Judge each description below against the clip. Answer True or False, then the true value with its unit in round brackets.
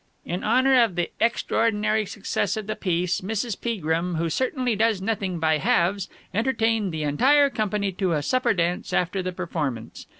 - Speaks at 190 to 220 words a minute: False (165 wpm)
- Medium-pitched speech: False (195 Hz)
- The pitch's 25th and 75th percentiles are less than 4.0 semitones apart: False (4.6 semitones)